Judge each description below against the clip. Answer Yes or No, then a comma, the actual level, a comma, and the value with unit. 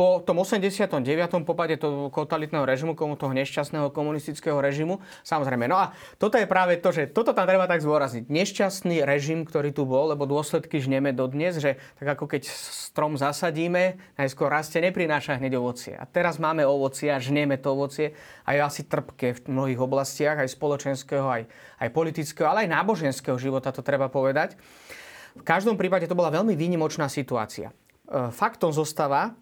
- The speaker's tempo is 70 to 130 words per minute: No, fast, 165 wpm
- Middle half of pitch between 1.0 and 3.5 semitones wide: No, average, 3.9 semitones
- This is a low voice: No, medium, 150 Hz